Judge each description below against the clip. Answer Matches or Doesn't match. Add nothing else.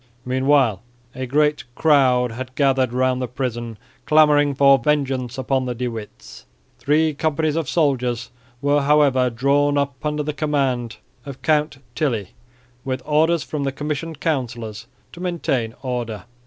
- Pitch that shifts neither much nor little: Matches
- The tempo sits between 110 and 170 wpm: Matches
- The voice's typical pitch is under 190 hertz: Matches